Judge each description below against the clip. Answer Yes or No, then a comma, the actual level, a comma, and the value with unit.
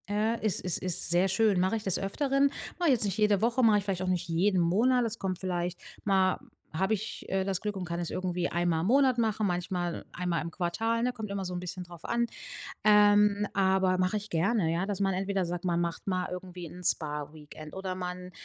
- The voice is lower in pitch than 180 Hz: No, high, 190 Hz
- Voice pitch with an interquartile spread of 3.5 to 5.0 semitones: No, average, 2.9 semitones